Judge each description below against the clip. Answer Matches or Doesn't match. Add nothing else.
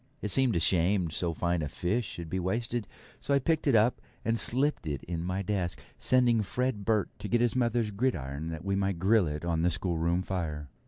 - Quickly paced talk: Matches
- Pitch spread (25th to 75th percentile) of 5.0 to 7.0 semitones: Matches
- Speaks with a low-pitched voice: Matches